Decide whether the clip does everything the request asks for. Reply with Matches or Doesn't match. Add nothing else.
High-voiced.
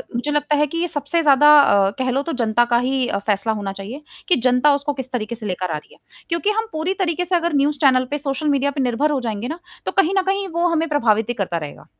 Matches